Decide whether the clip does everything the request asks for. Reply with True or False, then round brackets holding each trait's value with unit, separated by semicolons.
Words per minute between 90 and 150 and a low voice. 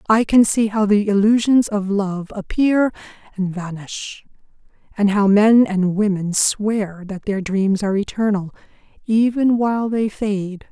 False (145 wpm; 205 Hz)